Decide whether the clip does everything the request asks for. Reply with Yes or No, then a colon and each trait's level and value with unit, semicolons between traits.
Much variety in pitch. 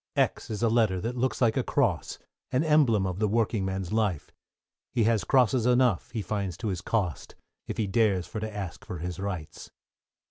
No: average, 3.7 semitones